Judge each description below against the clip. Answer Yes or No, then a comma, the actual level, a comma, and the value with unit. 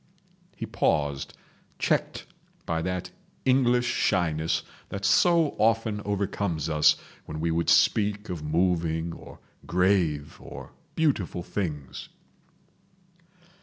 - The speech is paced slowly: Yes, slow, 105 wpm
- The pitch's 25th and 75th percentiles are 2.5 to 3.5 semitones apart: No, average, 4.4 semitones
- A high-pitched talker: No, very low, 90 Hz